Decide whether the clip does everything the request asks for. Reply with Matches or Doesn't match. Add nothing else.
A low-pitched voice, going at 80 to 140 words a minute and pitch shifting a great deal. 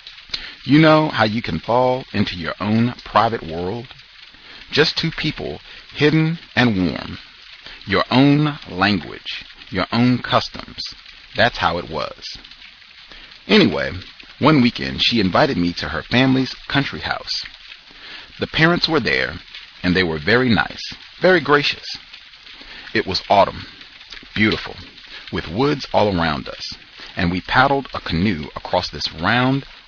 Matches